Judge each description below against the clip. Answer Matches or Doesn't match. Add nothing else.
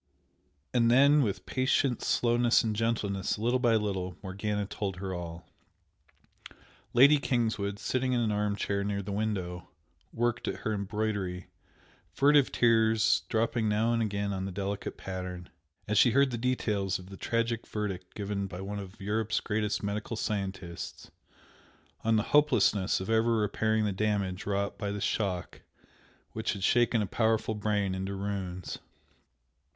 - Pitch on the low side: Matches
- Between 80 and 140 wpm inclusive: Doesn't match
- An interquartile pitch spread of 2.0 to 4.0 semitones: Matches